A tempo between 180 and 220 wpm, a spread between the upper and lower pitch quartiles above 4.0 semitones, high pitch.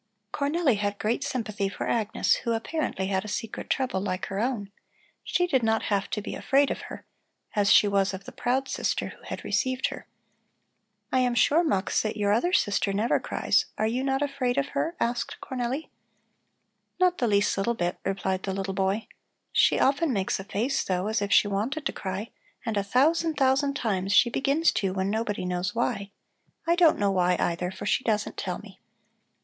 Yes: average, 195 wpm; average, 5.2 semitones; high, 220 Hz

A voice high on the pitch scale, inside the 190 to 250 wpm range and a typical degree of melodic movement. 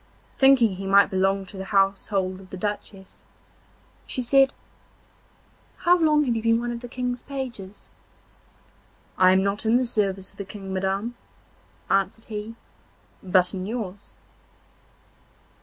No: high, 205 Hz; average, 140 wpm; average, 3.8 semitones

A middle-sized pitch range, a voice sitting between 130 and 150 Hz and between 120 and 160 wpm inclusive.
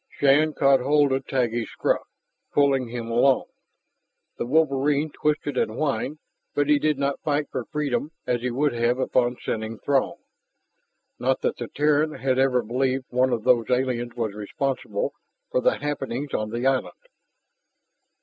Yes: average, 3.1 semitones; low, 135 Hz; average, 155 wpm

